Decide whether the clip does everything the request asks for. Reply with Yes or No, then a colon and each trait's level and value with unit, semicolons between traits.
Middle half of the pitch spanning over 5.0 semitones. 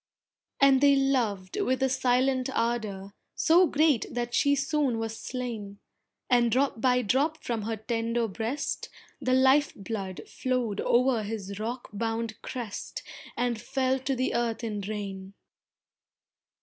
No: average, 3.3 semitones